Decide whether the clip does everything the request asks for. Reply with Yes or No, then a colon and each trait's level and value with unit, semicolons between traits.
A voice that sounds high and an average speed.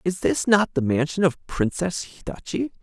No: medium, 155 Hz; average, 190 wpm